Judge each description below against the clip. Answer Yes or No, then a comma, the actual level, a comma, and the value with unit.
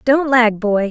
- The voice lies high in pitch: Yes, high, 235 Hz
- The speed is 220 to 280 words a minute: No, average, 200 wpm